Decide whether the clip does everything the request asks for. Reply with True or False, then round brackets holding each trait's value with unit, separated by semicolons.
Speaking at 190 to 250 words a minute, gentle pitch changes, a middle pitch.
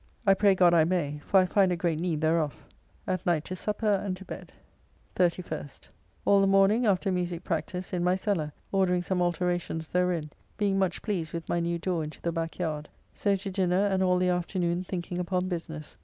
True (200 wpm; 2.1 semitones; 180 Hz)